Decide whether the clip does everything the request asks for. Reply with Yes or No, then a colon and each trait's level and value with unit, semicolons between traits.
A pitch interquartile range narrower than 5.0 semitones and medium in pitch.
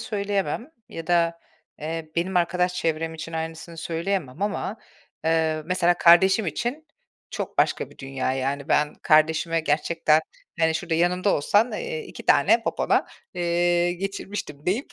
Yes: average, 2.9 semitones; medium, 170 Hz